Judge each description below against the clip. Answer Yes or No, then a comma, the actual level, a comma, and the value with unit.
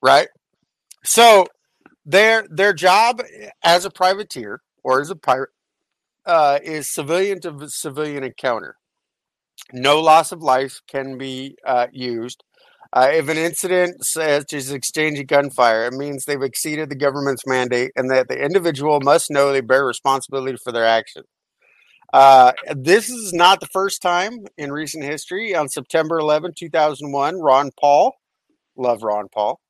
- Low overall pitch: No, medium, 145 Hz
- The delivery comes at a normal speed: Yes, average, 150 wpm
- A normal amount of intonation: Yes, average, 4.4 semitones